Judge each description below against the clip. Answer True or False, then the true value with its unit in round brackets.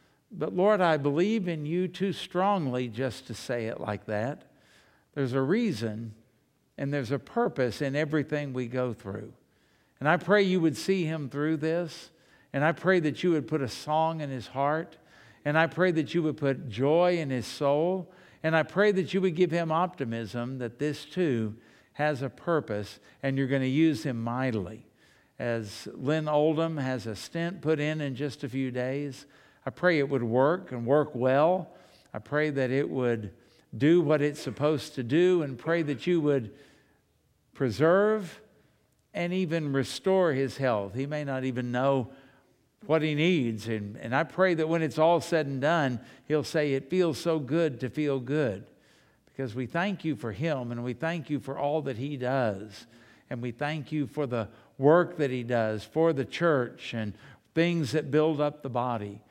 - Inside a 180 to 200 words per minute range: True (190 wpm)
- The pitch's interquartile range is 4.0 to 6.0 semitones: True (4.3 semitones)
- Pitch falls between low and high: True (145 Hz)